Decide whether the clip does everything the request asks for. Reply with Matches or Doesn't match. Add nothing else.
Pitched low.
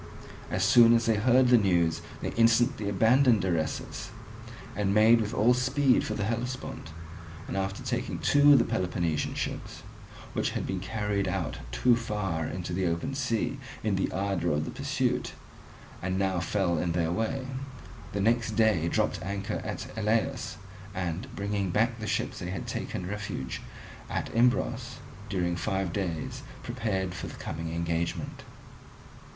Matches